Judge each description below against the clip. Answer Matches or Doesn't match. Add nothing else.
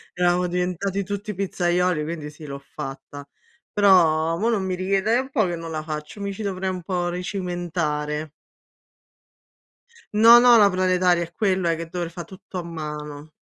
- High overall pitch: Doesn't match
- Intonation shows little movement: Doesn't match